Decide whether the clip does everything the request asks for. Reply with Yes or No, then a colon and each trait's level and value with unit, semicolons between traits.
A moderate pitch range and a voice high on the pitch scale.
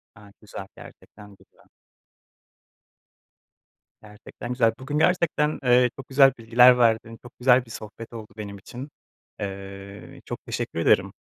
No: average, 3.3 semitones; low, 115 Hz